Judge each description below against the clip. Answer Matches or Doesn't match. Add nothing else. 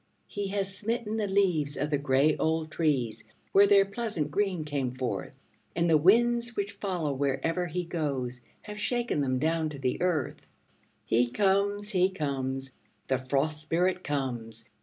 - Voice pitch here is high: Doesn't match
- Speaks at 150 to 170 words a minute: Matches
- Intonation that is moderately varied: Doesn't match